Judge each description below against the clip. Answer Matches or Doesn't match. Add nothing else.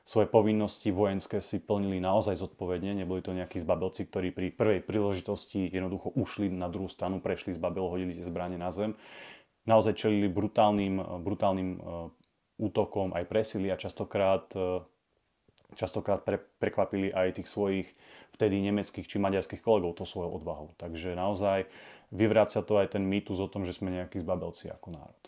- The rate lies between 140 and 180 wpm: Matches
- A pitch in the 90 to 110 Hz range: Matches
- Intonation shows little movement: Matches